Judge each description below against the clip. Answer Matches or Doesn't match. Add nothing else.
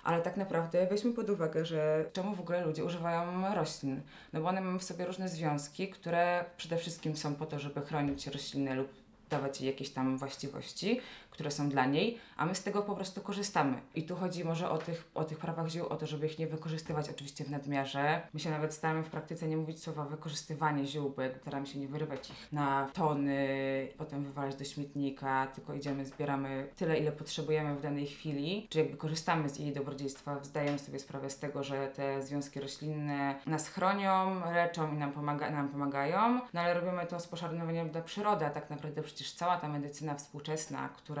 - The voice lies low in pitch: Doesn't match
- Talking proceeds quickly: Matches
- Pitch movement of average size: Matches